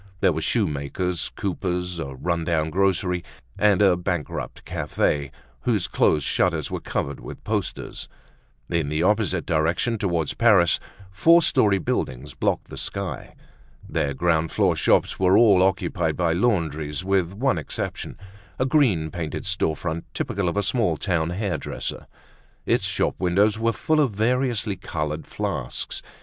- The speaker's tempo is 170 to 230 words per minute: No, average, 145 wpm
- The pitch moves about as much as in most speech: Yes, average, 4.2 semitones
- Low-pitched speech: Yes, very low, 90 Hz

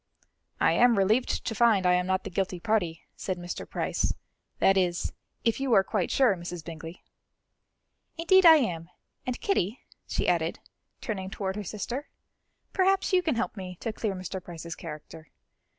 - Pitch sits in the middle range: No, high, 195 Hz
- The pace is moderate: Yes, average, 165 wpm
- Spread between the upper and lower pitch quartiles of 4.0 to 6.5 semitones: Yes, average, 5.1 semitones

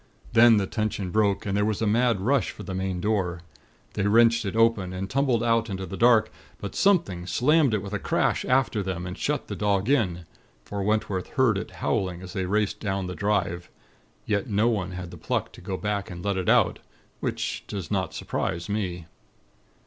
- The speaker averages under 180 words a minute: No, average, 200 wpm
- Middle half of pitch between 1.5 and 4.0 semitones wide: Yes, average, 3.3 semitones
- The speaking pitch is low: Yes, low, 100 Hz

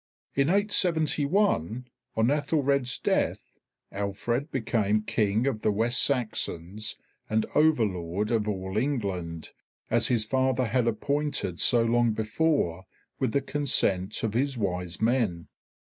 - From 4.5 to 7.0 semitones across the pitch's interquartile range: Yes, average, 5.2 semitones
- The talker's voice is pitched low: Yes, low, 115 Hz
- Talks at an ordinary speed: No, slow, 125 wpm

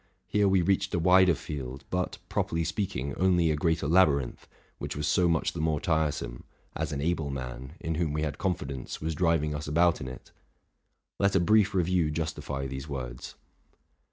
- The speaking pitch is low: Yes, very low, 80 Hz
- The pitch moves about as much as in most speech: Yes, average, 3.8 semitones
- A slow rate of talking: No, average, 175 wpm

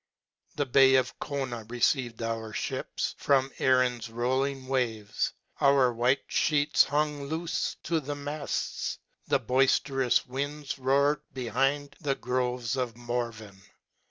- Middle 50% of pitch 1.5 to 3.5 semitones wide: Yes, average, 2.7 semitones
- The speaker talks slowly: Yes, slow, 125 wpm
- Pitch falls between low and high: No, low, 130 Hz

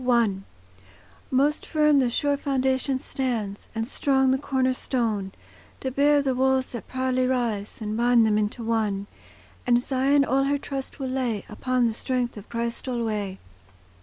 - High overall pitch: Yes, very high, 255 Hz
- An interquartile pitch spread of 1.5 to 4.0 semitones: Yes, average, 2.8 semitones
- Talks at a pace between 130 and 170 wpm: Yes, average, 160 wpm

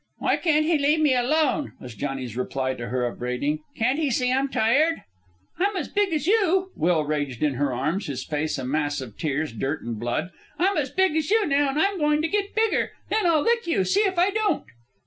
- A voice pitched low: No, very high, 270 Hz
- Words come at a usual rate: No, fast, 225 wpm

